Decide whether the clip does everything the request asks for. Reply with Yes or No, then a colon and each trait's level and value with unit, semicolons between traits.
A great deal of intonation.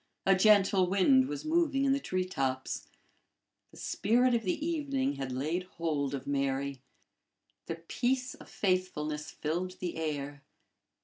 Yes: wide, 9.0 semitones